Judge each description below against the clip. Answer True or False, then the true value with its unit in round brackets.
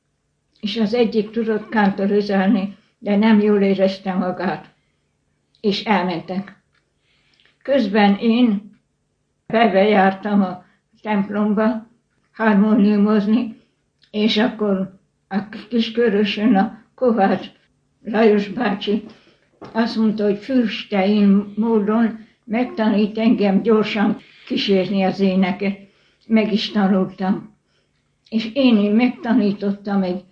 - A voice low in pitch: False (210 Hz)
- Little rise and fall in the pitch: True (2.2 semitones)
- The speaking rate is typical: False (90 wpm)